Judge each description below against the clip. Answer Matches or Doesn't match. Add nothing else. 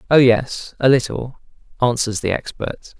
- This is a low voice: Matches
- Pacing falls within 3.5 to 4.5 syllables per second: Matches